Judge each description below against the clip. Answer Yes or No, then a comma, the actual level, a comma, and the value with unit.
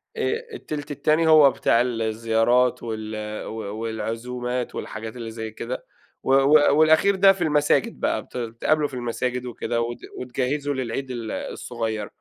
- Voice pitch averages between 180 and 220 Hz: No, low, 125 Hz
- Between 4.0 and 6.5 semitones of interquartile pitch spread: Yes, average, 4.4 semitones